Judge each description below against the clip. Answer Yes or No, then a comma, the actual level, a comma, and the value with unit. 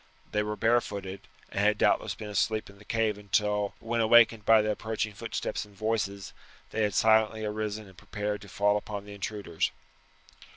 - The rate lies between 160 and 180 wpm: Yes, average, 175 wpm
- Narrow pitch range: Yes, narrow, 1.3 semitones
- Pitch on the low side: Yes, low, 105 Hz